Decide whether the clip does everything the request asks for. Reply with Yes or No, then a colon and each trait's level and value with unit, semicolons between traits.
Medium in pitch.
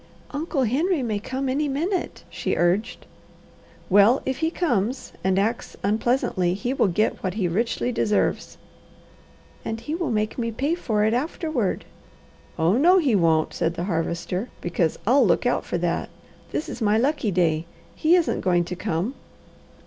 No: high, 225 Hz